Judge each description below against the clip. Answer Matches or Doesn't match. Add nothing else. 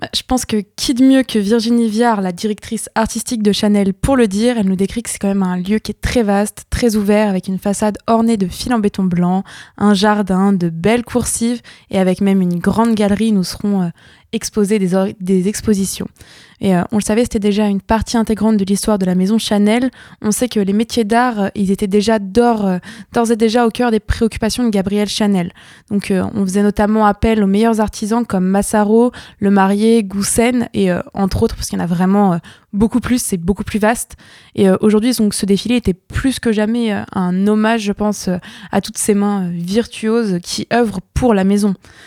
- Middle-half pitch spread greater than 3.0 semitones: Doesn't match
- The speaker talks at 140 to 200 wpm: Doesn't match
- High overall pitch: Matches